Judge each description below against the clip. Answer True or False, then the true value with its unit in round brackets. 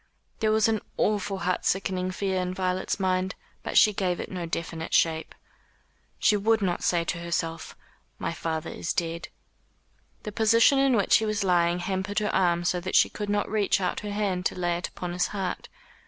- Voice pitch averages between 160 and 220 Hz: True (185 Hz)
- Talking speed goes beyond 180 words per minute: True (195 wpm)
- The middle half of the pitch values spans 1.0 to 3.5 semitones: True (2.9 semitones)